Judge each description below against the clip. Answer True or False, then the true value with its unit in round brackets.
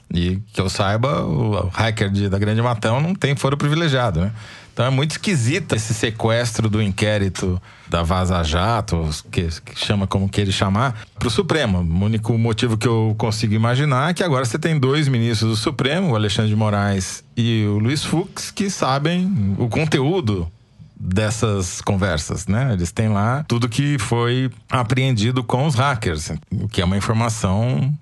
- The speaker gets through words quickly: False (175 wpm)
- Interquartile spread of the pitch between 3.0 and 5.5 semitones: True (4.5 semitones)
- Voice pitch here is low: True (115 Hz)